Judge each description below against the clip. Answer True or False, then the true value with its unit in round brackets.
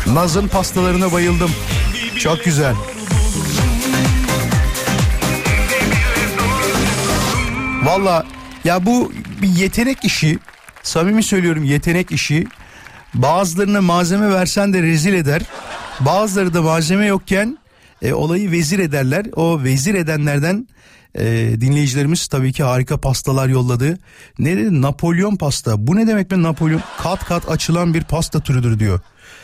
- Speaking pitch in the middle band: True (165 Hz)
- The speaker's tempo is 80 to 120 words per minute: True (110 wpm)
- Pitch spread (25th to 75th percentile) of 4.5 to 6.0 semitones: True (5.3 semitones)